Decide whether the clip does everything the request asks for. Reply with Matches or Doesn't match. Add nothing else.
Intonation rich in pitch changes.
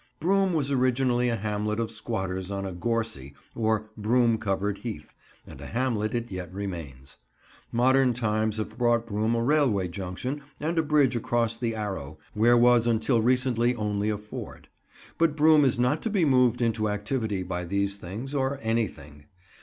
Doesn't match